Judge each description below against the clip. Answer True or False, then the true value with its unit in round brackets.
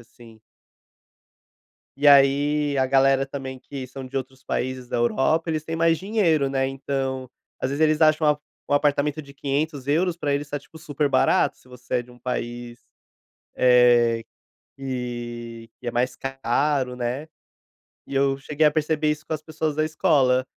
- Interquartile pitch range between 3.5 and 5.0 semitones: False (2.9 semitones)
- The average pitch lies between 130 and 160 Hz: True (135 Hz)